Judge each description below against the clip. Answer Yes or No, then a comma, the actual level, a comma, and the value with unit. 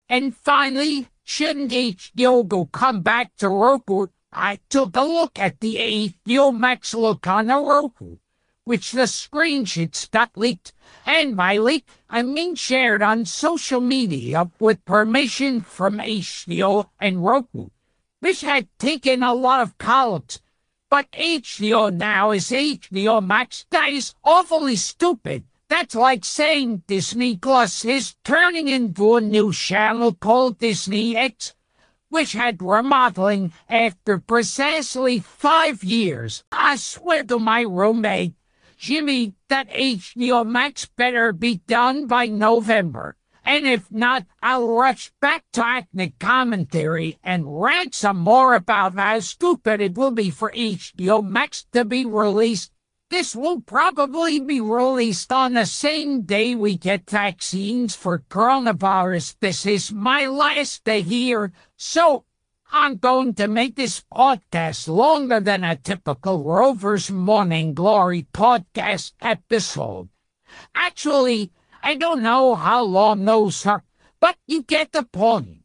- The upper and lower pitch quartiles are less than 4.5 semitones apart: No, average, 4.8 semitones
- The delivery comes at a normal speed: No, slow, 130 wpm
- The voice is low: No, high, 230 Hz